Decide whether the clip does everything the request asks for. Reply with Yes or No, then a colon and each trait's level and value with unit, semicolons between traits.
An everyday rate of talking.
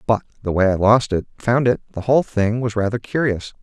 Yes: average, 180 wpm